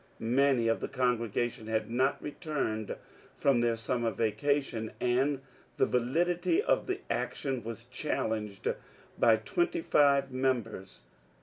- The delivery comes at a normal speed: No, slow, 120 wpm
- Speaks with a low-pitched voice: Yes, low, 125 Hz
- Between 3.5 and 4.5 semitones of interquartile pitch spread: Yes, average, 3.8 semitones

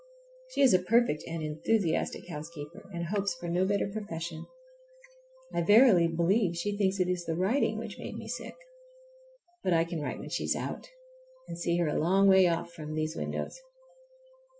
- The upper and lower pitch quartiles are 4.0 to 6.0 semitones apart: No, average, 3.3 semitones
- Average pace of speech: Yes, average, 180 wpm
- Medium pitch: Yes, medium, 175 Hz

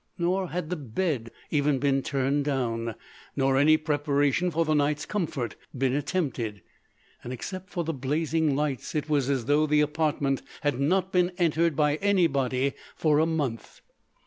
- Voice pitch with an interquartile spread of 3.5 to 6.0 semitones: No, average, 3.1 semitones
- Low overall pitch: No, medium, 145 Hz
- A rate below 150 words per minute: No, average, 155 wpm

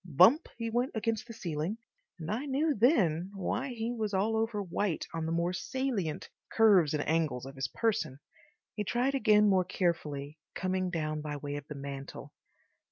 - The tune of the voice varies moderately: No, wide, 6.5 semitones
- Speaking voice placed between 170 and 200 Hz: Yes, high, 190 Hz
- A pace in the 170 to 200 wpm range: Yes, average, 175 wpm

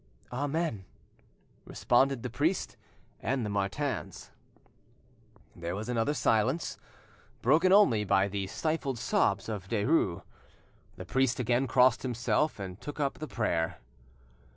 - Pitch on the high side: No, low, 125 Hz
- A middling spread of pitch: No, wide, 5.8 semitones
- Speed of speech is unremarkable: No, slow, 120 wpm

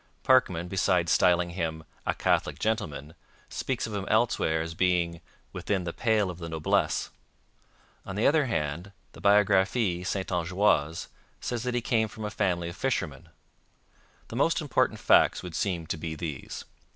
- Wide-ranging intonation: No, average, 4.2 semitones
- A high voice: No, very low, 90 Hz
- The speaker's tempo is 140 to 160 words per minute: Yes, average, 155 wpm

